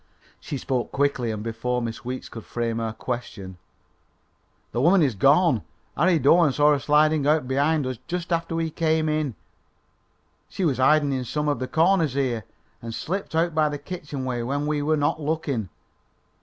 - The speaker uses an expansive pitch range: No, average, 4.1 semitones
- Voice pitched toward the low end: No, medium, 145 Hz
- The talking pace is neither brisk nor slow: Yes, average, 180 wpm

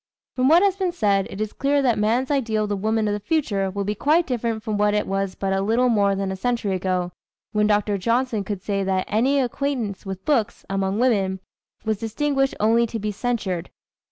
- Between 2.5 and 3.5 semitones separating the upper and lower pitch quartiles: No, average, 3.9 semitones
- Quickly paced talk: Yes, fast, 215 wpm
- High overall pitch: Yes, high, 215 Hz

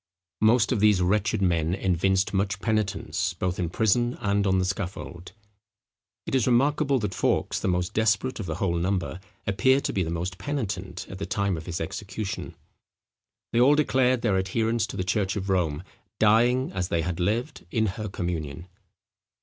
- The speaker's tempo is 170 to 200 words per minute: Yes, average, 175 wpm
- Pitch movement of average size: Yes, average, 3.6 semitones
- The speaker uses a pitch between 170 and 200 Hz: No, low, 100 Hz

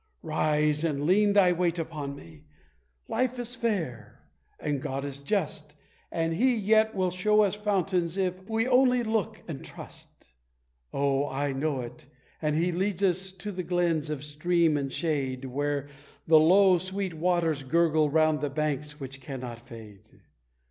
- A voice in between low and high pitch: Yes, medium, 165 Hz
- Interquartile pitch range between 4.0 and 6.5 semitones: Yes, average, 4.7 semitones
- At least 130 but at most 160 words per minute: Yes, average, 155 wpm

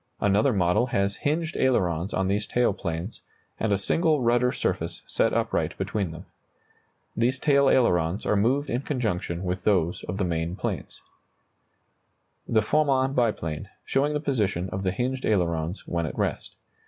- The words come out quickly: No, average, 160 wpm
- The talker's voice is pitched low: Yes, low, 105 Hz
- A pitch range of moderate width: No, wide, 6.4 semitones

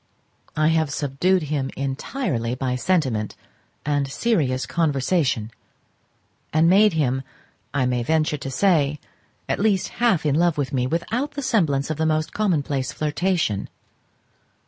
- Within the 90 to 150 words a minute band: Yes, slow, 135 wpm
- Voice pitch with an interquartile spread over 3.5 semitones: Yes, average, 4.6 semitones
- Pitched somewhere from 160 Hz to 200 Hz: No, medium, 150 Hz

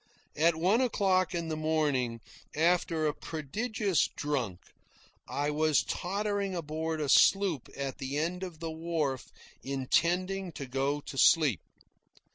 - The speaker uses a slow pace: Yes, slow, 130 wpm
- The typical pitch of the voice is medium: Yes, medium, 160 Hz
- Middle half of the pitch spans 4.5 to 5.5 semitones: No, average, 4.1 semitones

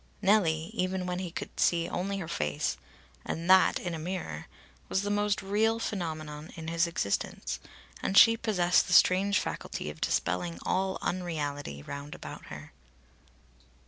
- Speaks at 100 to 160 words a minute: Yes, average, 150 wpm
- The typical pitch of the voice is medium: Yes, medium, 175 Hz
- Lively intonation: No, average, 3.7 semitones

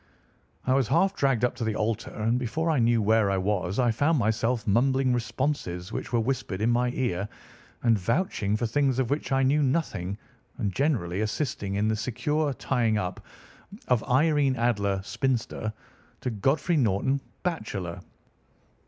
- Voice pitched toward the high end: No, low, 120 Hz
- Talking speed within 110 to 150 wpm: No, average, 160 wpm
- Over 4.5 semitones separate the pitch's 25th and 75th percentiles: No, average, 4.2 semitones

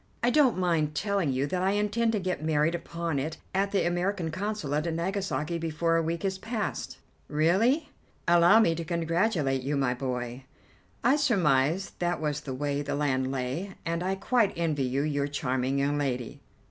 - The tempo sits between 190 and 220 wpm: No, average, 180 wpm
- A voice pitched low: No, medium, 165 Hz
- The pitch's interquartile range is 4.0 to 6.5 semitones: Yes, average, 5.1 semitones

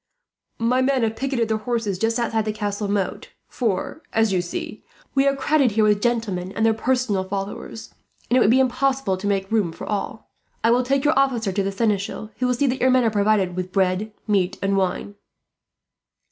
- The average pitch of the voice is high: Yes, high, 220 Hz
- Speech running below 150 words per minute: No, fast, 205 wpm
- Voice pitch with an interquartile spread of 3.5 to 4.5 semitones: Yes, average, 4.0 semitones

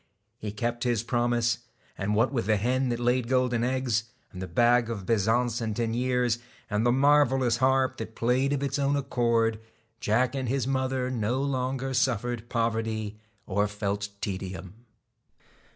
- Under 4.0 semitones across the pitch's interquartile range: Yes, narrow, 2.6 semitones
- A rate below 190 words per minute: Yes, average, 155 wpm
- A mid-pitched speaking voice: No, low, 120 Hz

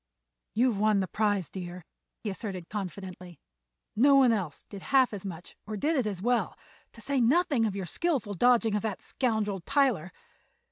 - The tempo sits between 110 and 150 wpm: No, average, 175 wpm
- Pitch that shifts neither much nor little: Yes, average, 4.6 semitones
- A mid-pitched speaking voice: No, high, 210 Hz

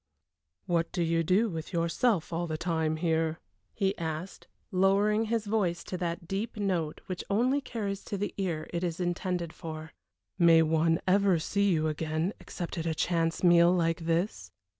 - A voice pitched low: No, medium, 170 Hz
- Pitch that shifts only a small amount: No, average, 3.1 semitones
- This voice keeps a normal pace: Yes, average, 170 wpm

